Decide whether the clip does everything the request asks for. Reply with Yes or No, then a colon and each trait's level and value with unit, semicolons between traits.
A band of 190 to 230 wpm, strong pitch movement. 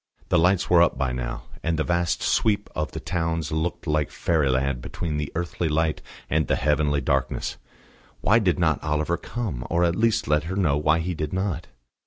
No: average, 195 wpm; average, 2.8 semitones